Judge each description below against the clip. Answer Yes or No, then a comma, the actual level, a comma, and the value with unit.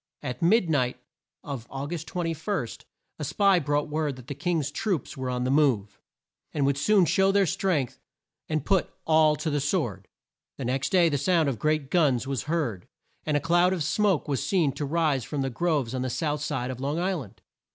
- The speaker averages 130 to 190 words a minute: No, fast, 205 wpm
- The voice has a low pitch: No, medium, 150 Hz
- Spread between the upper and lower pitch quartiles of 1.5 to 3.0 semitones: No, average, 4.2 semitones